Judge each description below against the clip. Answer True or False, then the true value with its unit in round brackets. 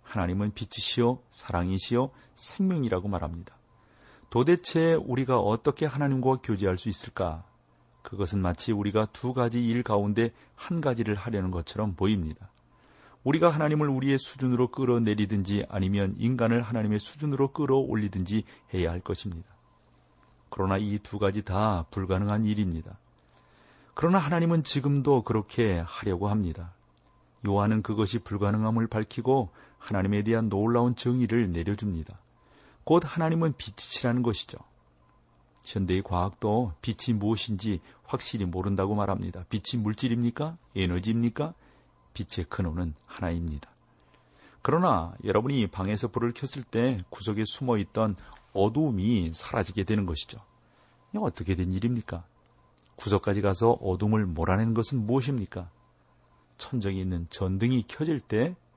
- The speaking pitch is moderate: False (105 Hz)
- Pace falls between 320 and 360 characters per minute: True (325 characters per minute)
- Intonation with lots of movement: False (4.4 semitones)